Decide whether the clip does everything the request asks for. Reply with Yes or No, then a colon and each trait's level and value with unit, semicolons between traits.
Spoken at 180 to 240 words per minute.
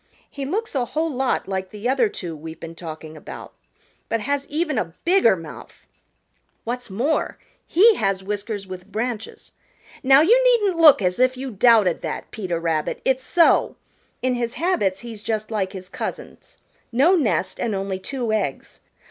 No: average, 165 wpm